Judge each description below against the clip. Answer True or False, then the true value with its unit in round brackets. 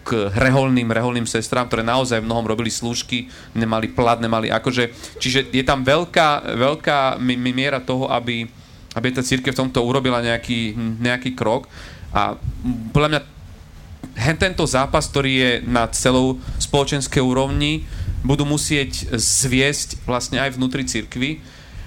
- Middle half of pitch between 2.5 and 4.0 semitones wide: True (2.9 semitones)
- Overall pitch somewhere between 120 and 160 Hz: True (125 Hz)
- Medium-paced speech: True (135 wpm)